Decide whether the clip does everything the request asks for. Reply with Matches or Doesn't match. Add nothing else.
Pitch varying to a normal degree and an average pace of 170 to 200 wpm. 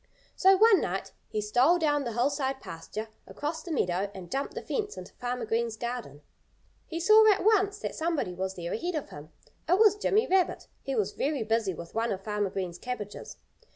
Doesn't match